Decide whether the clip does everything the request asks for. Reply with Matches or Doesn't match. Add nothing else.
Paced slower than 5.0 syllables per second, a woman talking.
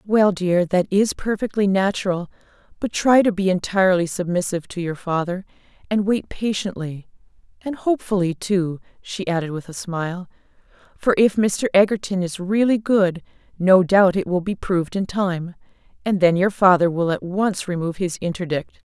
Doesn't match